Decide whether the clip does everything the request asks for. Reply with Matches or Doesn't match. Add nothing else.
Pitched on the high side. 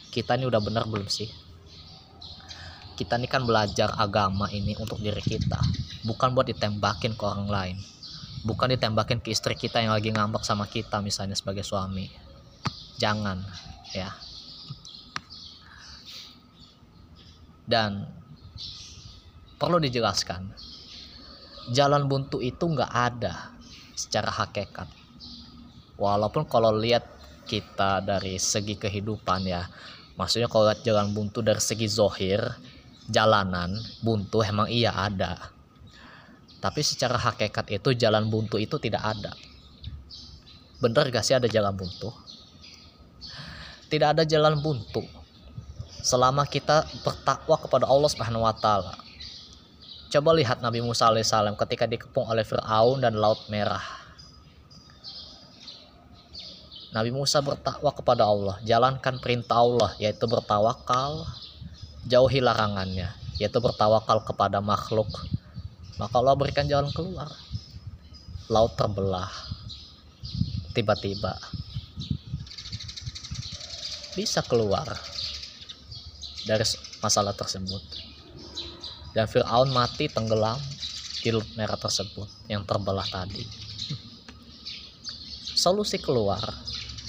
Doesn't match